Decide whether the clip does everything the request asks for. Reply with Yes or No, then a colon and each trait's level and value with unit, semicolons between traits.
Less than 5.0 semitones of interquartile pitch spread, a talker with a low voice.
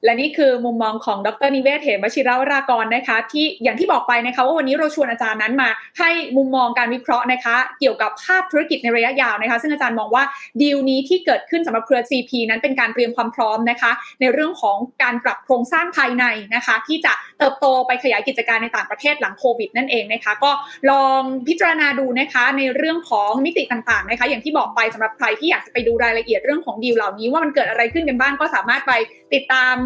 No: average, 3.2 semitones; very high, 255 Hz